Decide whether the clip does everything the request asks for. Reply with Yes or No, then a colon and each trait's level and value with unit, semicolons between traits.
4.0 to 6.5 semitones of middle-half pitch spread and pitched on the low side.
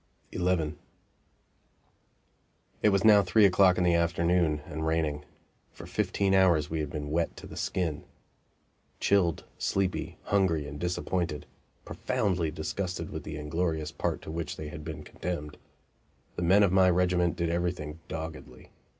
No: average, 2.8 semitones; very low, 85 Hz